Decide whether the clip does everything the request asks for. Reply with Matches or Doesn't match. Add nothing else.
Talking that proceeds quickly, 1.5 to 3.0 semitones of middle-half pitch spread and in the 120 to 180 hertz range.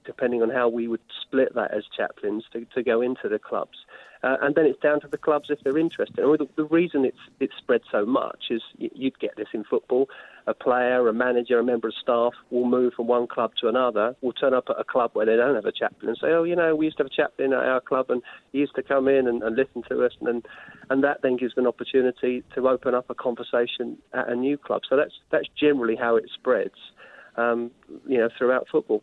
Matches